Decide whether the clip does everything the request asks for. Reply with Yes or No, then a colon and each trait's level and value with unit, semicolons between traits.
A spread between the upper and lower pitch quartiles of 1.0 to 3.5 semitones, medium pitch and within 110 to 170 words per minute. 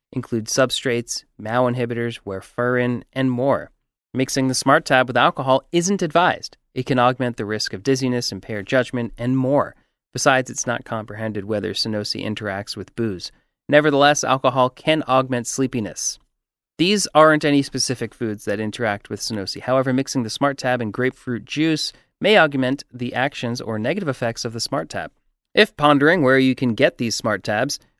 No: average, 2.7 semitones; low, 125 Hz; average, 165 wpm